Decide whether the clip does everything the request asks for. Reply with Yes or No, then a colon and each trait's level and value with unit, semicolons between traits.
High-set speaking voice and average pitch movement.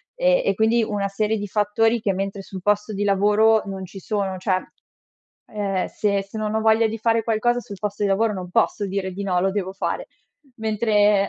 No: high, 205 Hz; narrow, 2.0 semitones